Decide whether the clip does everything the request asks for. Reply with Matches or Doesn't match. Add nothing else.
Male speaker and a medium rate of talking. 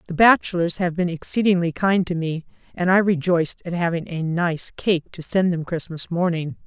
Doesn't match